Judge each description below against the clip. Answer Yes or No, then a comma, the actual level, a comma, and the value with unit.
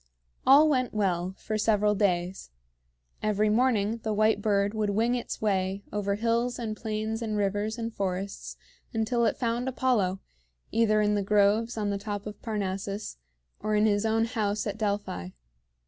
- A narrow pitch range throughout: Yes, narrow, 2.0 semitones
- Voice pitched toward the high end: Yes, high, 210 Hz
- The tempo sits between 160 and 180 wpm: Yes, average, 165 wpm